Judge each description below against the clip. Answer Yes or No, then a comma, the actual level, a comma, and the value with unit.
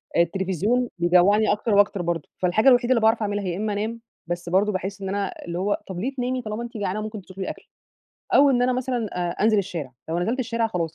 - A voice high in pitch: Yes, high, 205 Hz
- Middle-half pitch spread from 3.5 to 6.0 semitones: Yes, average, 4.2 semitones